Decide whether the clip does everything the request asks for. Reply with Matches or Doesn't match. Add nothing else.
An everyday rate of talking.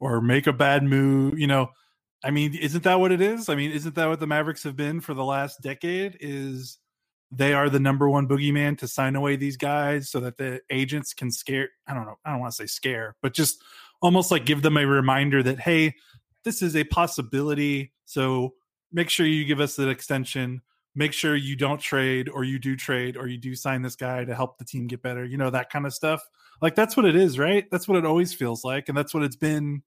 Doesn't match